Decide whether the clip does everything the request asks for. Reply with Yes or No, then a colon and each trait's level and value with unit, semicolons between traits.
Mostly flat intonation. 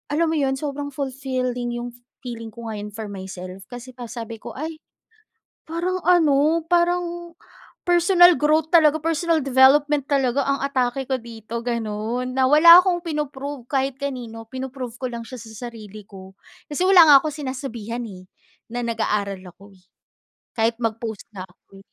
No: average, 4.8 semitones